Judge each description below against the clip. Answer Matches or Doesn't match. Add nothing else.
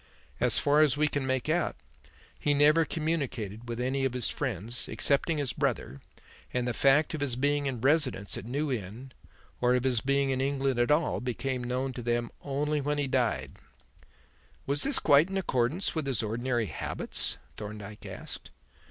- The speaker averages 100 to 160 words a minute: Doesn't match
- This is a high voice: Doesn't match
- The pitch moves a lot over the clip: Doesn't match